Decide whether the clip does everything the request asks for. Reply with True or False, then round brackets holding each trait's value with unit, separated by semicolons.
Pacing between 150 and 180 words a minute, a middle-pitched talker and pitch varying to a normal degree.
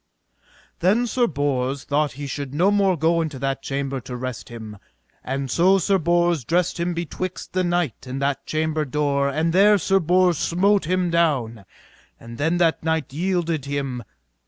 True (170 wpm; 160 Hz; 4.4 semitones)